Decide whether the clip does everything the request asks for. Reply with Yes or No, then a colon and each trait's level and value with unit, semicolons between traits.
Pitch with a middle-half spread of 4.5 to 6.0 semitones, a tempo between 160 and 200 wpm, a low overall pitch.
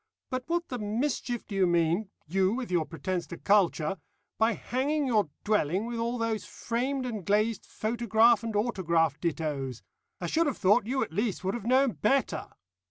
No: average, 4.8 semitones; average, 175 wpm; high, 215 Hz